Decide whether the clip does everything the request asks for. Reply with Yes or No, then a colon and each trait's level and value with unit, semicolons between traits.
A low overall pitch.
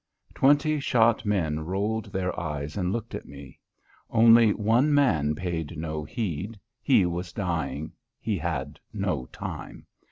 Yes: very low, 90 Hz